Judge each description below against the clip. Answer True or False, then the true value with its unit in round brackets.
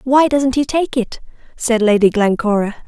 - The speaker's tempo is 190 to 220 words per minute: False (165 wpm)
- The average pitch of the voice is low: False (240 Hz)